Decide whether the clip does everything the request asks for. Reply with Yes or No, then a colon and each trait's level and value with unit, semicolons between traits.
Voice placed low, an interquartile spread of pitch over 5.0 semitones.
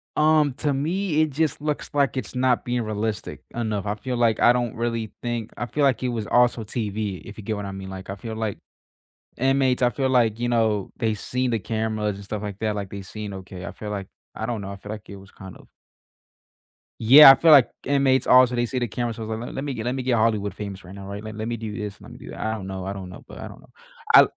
No: low, 110 Hz; average, 3.6 semitones